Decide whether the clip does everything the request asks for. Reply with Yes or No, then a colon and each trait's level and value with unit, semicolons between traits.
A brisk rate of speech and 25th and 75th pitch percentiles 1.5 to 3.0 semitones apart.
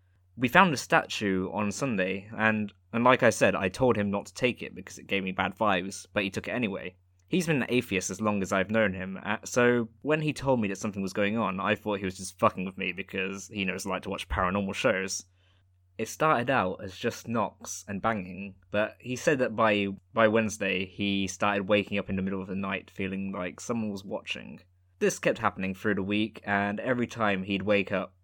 Yes: fast, 230 wpm; narrow, 2.4 semitones